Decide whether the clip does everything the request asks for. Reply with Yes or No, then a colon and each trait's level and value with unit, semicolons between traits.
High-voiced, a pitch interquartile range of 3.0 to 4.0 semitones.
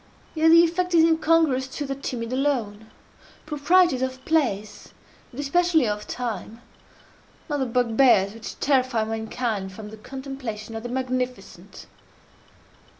No: very high, 255 Hz; average, 4.7 semitones